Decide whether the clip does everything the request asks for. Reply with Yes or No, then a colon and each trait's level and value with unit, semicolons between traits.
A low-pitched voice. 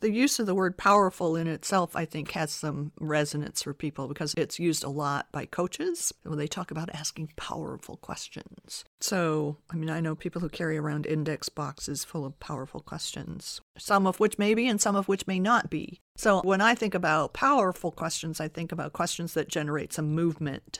No: medium, 165 Hz